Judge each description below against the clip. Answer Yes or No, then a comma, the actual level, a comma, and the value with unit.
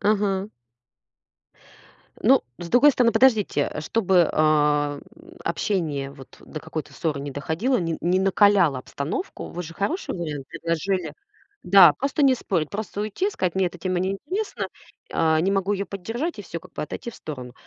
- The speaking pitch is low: No, medium, 185 Hz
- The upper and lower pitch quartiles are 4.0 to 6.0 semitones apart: Yes, average, 4.9 semitones